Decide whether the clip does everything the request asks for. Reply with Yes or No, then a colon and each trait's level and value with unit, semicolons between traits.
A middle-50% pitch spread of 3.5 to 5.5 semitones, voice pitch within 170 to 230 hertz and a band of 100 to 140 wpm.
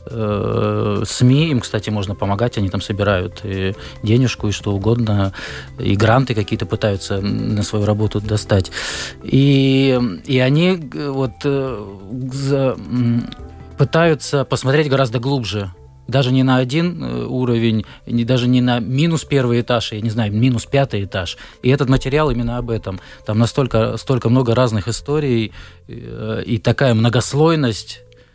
No: average, 3.9 semitones; low, 120 Hz; average, 130 wpm